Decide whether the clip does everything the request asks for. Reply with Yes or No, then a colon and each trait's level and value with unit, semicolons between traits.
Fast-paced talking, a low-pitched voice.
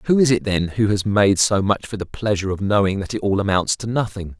Yes: fast, 275 wpm; low, 100 Hz